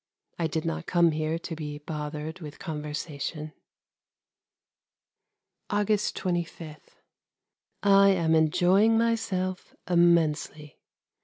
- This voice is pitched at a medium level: Yes, medium, 165 Hz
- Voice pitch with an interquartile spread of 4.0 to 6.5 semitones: No, average, 3.4 semitones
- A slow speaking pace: Yes, slow, 90 wpm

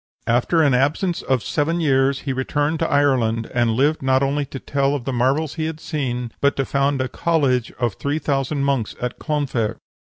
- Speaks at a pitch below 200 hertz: Yes, medium, 140 Hz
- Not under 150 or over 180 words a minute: No, average, 195 wpm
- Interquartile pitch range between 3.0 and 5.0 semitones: No, narrow, 2.5 semitones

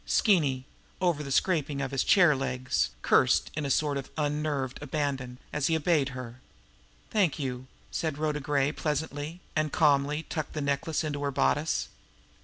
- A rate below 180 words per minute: Yes, average, 160 wpm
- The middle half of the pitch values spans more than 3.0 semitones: No, narrow, 2.4 semitones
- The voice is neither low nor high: Yes, medium, 145 Hz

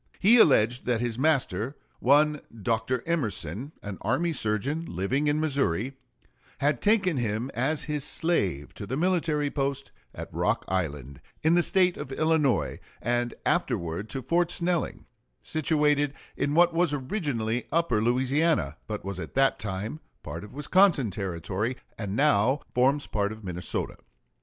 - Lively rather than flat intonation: Yes, wide, 6.4 semitones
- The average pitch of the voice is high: No, low, 135 Hz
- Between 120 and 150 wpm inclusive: Yes, average, 145 wpm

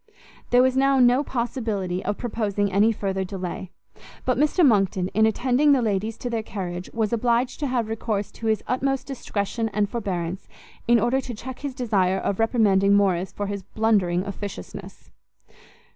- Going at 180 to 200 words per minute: No, average, 165 wpm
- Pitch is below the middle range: No, high, 220 Hz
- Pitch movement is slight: No, average, 3.9 semitones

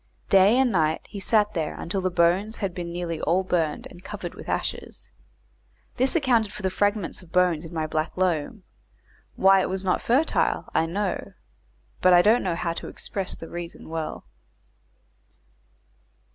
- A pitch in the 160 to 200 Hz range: Yes, medium, 185 Hz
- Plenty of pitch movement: No, average, 3.3 semitones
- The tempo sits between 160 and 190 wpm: Yes, average, 170 wpm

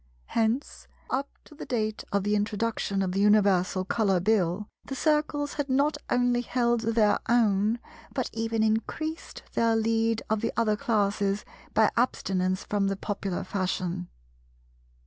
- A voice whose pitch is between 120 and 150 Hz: No, high, 220 Hz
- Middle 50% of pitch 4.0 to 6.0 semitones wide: No, average, 3.1 semitones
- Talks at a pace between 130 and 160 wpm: Yes, average, 145 wpm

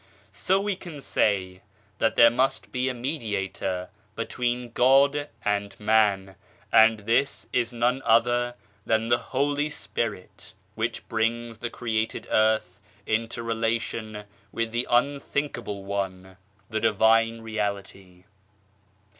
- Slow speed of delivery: Yes, slow, 120 wpm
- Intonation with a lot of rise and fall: No, average, 2.8 semitones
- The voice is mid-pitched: No, low, 115 Hz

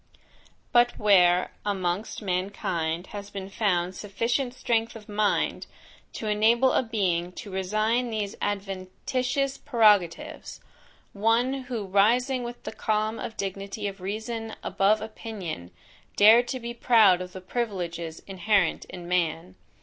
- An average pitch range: Yes, average, 3.7 semitones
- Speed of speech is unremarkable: No, slow, 125 wpm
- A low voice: No, high, 210 Hz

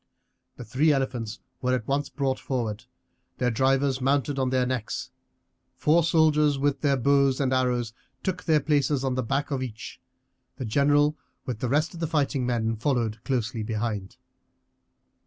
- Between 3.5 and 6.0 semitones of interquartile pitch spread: No, average, 2.9 semitones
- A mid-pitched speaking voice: No, low, 130 Hz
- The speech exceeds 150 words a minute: Yes, average, 160 wpm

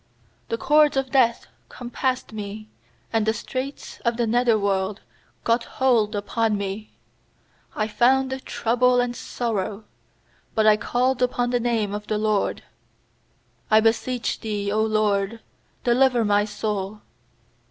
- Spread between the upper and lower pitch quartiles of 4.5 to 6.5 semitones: No, average, 2.7 semitones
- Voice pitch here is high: Yes, high, 225 Hz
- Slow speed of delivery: Yes, slow, 130 wpm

